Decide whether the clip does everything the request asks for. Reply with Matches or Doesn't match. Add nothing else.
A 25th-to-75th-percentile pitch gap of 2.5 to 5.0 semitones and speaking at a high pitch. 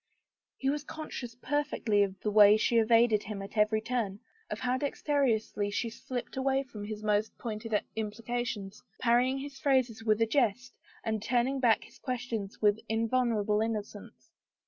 Matches